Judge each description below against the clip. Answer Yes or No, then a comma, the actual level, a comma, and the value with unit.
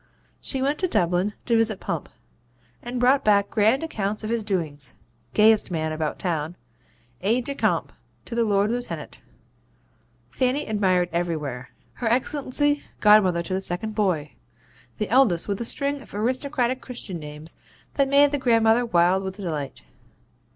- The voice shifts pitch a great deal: Yes, wide, 5.9 semitones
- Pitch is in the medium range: No, high, 215 Hz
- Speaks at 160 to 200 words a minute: No, average, 150 wpm